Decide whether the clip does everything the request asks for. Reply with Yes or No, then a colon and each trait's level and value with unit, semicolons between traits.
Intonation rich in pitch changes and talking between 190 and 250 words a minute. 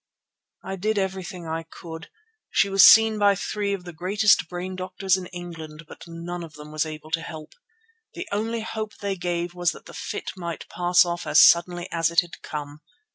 No: average, 2.7 semitones; average, 195 wpm